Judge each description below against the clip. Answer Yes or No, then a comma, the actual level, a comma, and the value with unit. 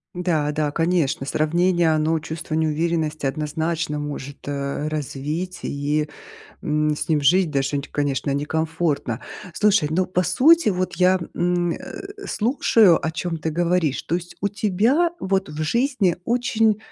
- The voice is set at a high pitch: No, medium, 165 Hz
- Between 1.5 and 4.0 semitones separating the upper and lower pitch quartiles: Yes, average, 3.6 semitones